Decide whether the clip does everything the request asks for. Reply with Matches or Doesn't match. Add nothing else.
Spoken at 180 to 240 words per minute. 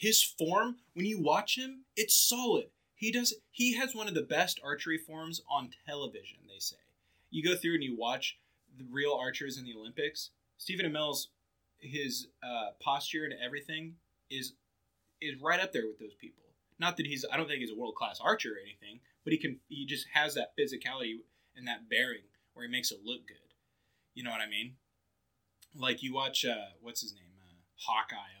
Matches